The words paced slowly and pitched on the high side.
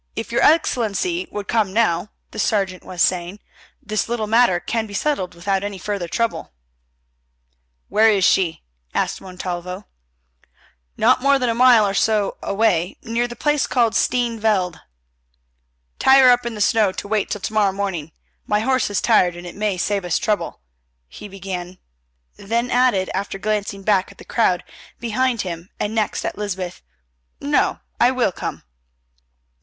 No: average, 165 wpm; high, 210 Hz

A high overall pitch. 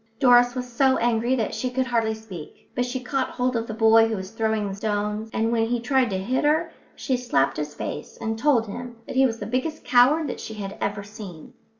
Yes: high, 230 Hz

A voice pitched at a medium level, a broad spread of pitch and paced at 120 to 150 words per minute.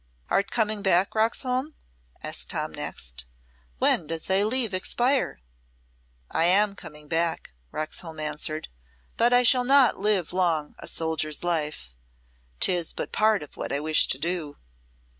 Yes: medium, 175 Hz; wide, 6.0 semitones; average, 140 wpm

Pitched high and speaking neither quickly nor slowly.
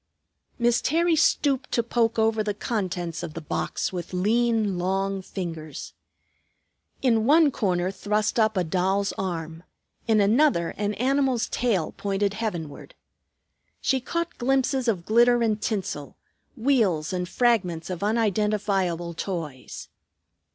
No: high, 210 Hz; slow, 125 wpm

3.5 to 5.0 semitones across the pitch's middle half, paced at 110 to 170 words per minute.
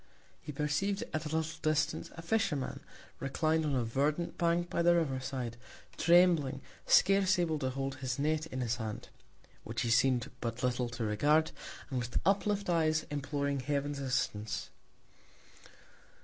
Yes: average, 4.1 semitones; average, 150 wpm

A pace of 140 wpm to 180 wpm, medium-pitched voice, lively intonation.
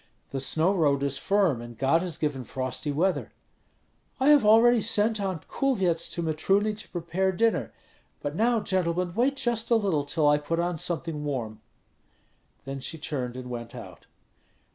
Yes: average, 165 wpm; medium, 170 Hz; wide, 6.5 semitones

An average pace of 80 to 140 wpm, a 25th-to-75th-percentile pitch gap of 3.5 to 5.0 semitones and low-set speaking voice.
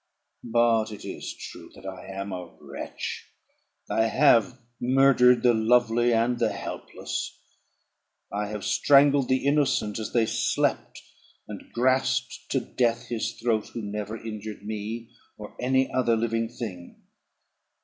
No: slow, 135 wpm; narrow, 2.6 semitones; low, 115 Hz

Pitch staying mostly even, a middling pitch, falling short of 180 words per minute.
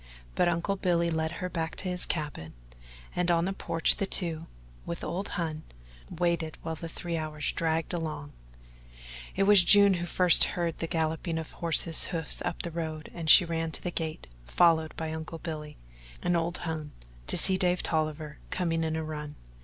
No: narrow, 1.7 semitones; medium, 165 Hz; average, 195 wpm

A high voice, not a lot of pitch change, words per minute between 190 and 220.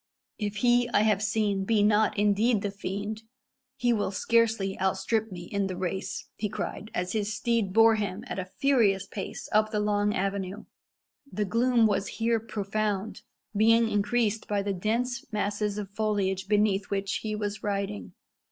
No: high, 210 Hz; narrow, 1.9 semitones; average, 165 wpm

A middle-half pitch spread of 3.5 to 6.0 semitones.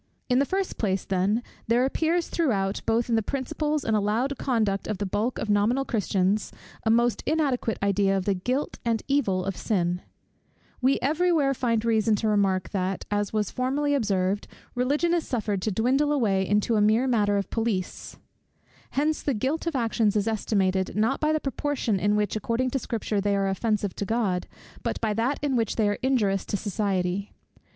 Yes: average, 4.5 semitones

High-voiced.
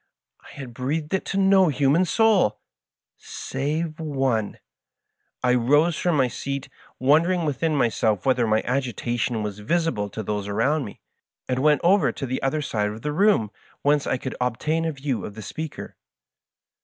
No: low, 135 Hz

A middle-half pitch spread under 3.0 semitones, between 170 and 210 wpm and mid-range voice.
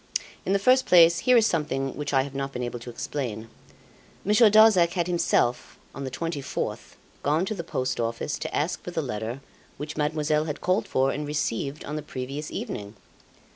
No: average, 4.6 semitones; average, 190 wpm; medium, 150 Hz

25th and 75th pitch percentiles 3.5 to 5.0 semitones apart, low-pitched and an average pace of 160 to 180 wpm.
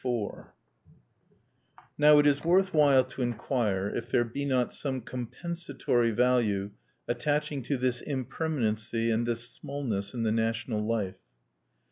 No: average, 3.8 semitones; low, 125 Hz; slow, 135 wpm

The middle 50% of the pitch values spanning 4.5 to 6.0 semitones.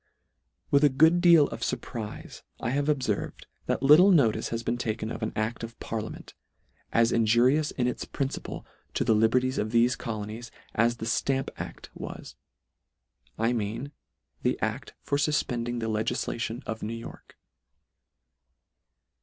No: average, 3.3 semitones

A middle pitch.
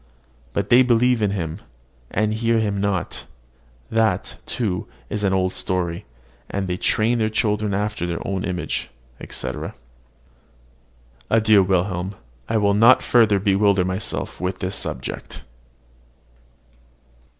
No: low, 100 Hz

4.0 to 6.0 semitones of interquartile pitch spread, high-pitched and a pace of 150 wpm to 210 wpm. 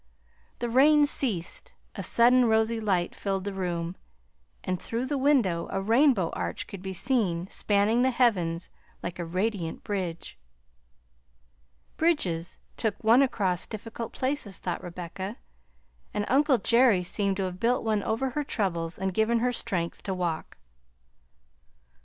No: average, 5.1 semitones; high, 205 Hz; average, 140 wpm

